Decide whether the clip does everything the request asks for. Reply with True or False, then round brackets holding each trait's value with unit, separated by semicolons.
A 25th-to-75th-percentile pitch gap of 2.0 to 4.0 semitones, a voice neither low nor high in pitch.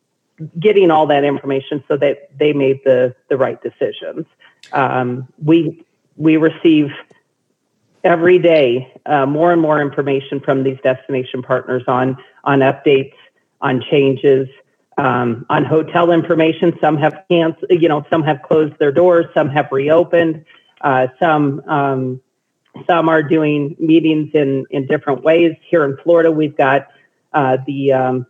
True (3.3 semitones; 150 Hz)